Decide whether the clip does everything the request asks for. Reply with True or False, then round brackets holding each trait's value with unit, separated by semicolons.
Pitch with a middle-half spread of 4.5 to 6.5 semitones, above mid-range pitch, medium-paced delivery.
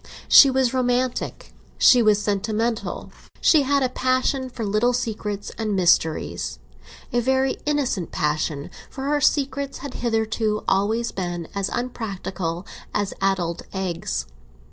False (5.1 semitones; 220 Hz; 120 wpm)